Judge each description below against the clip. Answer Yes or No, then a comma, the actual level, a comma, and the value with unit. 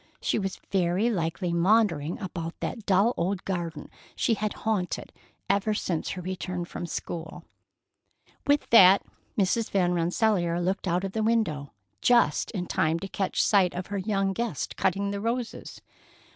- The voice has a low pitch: No, high, 190 Hz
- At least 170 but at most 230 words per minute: No, average, 155 wpm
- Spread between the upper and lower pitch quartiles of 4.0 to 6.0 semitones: No, average, 3.5 semitones